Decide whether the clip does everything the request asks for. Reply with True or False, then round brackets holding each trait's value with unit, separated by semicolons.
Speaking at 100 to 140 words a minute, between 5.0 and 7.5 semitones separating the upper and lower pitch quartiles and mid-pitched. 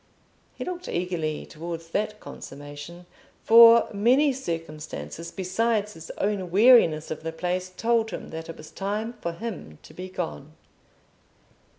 True (135 wpm; 5.3 semitones; 180 Hz)